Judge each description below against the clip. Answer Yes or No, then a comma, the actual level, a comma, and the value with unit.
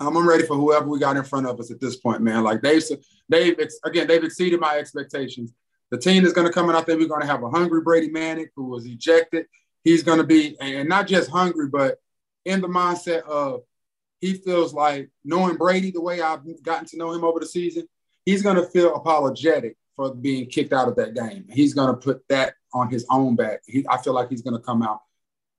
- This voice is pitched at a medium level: Yes, medium, 160 Hz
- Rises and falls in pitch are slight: No, average, 3.8 semitones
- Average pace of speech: No, fast, 235 wpm